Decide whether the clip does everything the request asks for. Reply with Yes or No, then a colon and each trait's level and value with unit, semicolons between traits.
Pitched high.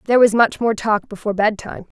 Yes: high, 215 Hz